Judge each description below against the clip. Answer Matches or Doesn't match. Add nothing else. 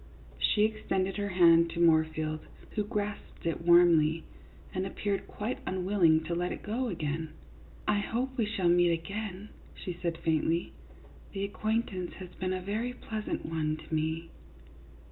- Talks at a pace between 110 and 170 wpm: Matches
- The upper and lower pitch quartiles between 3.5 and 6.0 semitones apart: Matches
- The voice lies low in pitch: Doesn't match